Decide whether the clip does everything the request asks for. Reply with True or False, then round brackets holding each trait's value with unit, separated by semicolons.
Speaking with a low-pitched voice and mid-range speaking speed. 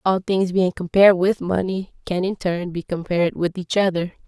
False (185 Hz; 195 wpm)